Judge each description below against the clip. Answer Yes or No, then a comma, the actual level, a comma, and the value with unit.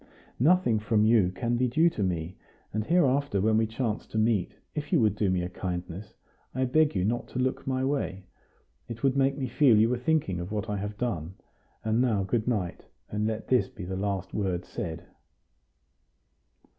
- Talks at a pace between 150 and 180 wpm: No, average, 195 wpm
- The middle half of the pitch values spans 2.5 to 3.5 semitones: No, average, 4.8 semitones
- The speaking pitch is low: Yes, low, 110 Hz